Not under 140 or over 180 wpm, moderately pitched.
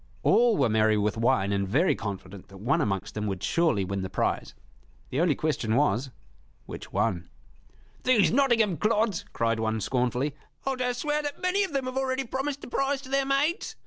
No: average, 190 wpm; medium, 155 Hz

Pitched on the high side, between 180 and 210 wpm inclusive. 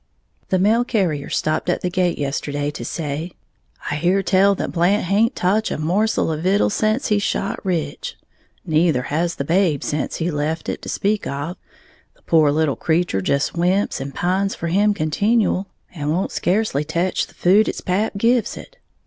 No: medium, 175 Hz; average, 185 wpm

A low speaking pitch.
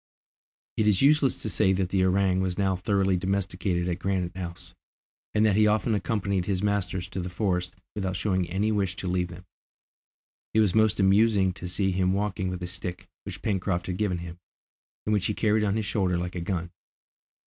Yes: very low, 95 Hz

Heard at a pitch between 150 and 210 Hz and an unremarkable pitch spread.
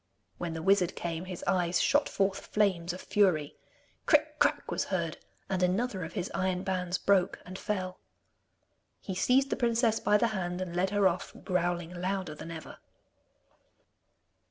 No: medium, 185 Hz; narrow, 2.2 semitones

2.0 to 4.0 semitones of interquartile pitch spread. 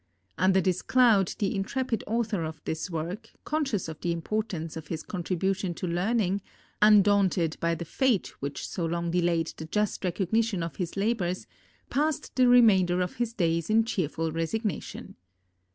No: average, 4.5 semitones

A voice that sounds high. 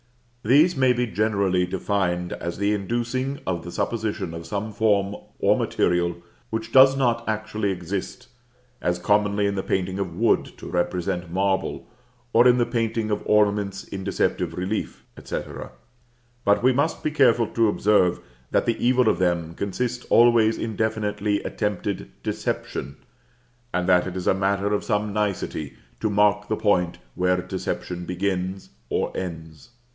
No: low, 100 Hz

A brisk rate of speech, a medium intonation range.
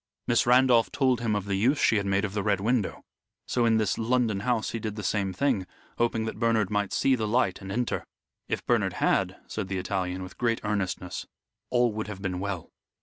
Yes: fast, 215 wpm; average, 3.2 semitones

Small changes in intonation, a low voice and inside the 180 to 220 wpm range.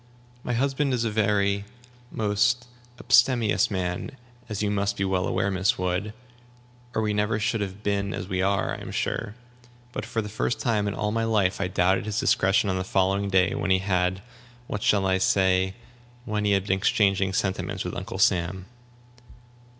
Yes: narrow, 2.1 semitones; low, 100 Hz; average, 185 wpm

